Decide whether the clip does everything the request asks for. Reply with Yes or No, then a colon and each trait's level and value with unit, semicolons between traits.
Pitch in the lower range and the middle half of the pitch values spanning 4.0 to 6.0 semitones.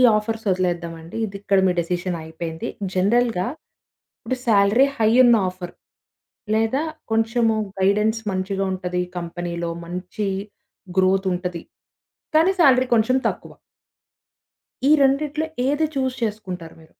No: high, 200 Hz; average, 4.5 semitones